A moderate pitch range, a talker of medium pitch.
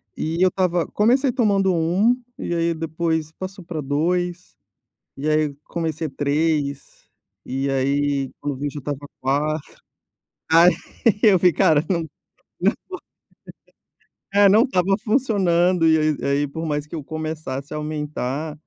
Yes: average, 3.5 semitones; medium, 160 Hz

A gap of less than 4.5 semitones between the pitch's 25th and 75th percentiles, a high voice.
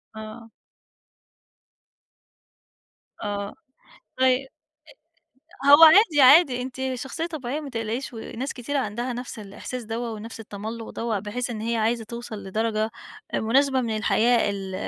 Yes: average, 3.1 semitones; high, 235 Hz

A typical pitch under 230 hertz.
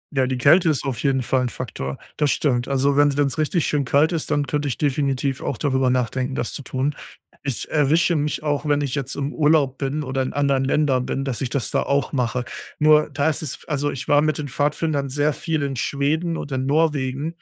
Yes: medium, 140 Hz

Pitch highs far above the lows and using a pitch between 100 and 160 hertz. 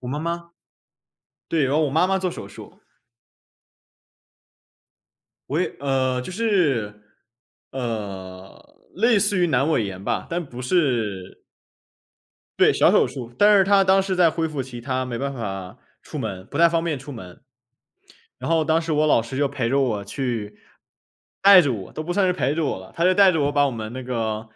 Yes: wide, 6.6 semitones; medium, 140 Hz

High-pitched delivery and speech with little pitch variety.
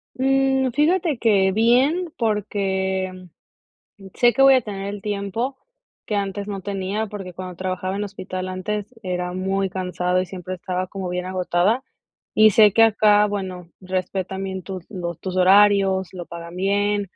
Yes: high, 195 Hz; narrow, 2.3 semitones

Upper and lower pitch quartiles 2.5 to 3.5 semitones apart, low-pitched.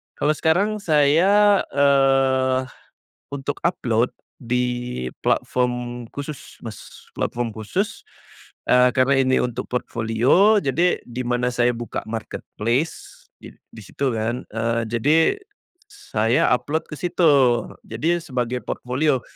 No: average, 3.9 semitones; low, 130 Hz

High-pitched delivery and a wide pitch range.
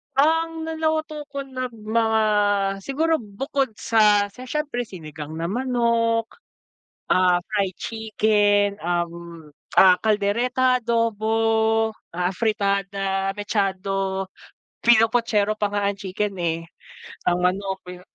No: high, 210 Hz; average, 3.8 semitones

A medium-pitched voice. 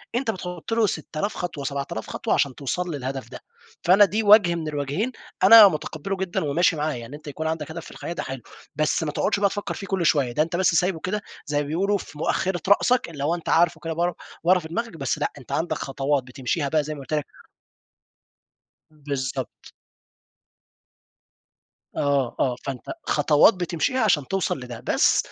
Yes: medium, 160 Hz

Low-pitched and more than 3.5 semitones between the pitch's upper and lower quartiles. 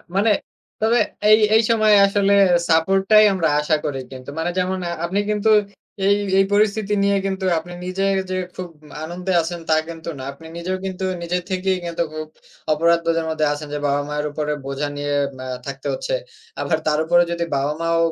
No: medium, 170 Hz; average, 3.9 semitones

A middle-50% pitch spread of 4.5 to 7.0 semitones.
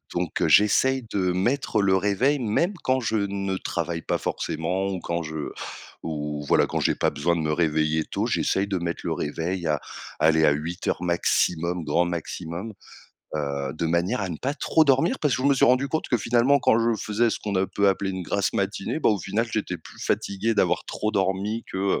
Yes: average, 5.0 semitones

